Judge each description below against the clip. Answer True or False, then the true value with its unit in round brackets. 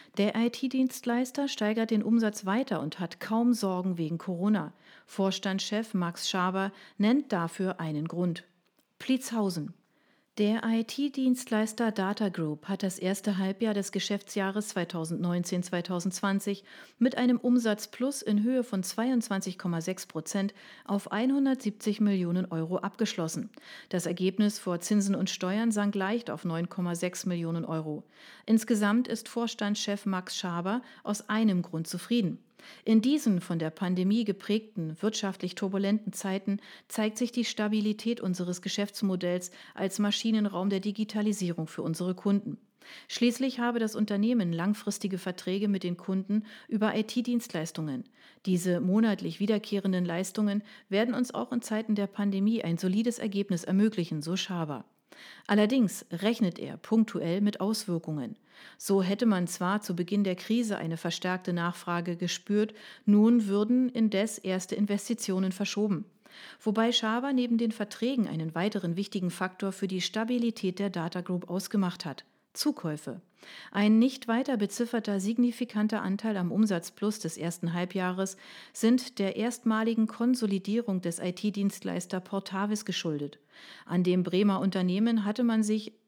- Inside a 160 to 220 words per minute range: False (130 wpm)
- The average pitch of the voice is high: True (205 Hz)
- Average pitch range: True (3.3 semitones)